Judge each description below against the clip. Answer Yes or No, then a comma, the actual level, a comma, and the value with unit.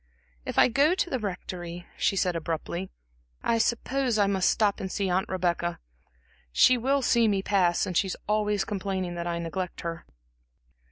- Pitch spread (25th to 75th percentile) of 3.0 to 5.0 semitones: Yes, average, 3.6 semitones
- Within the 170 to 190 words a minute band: Yes, average, 175 wpm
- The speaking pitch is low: No, high, 190 Hz